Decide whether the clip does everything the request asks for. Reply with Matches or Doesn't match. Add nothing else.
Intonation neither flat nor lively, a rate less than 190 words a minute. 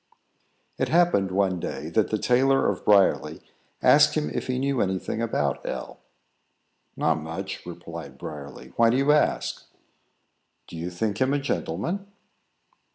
Doesn't match